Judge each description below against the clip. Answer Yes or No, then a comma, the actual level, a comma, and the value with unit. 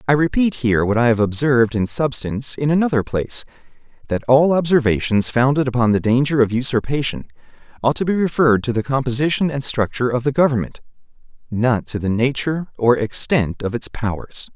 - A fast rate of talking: No, average, 175 wpm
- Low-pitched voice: Yes, low, 130 Hz